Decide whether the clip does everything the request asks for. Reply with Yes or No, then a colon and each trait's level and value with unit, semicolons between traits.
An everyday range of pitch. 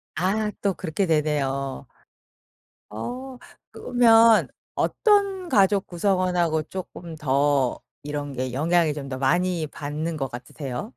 No: wide, 5.7 semitones